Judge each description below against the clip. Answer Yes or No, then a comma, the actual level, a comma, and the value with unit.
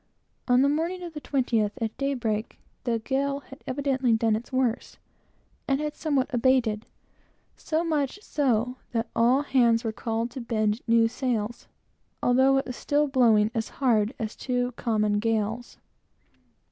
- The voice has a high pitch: Yes, high, 245 Hz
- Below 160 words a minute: Yes, average, 150 wpm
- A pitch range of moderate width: Yes, average, 3.2 semitones